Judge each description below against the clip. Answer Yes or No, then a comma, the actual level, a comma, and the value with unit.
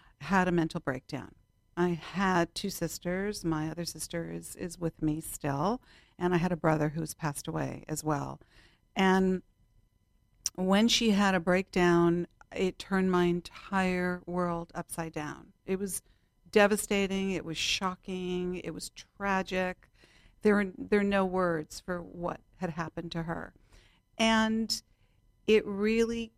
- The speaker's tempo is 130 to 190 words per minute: Yes, average, 140 wpm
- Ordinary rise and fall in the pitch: Yes, average, 3.4 semitones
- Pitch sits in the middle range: Yes, medium, 180 Hz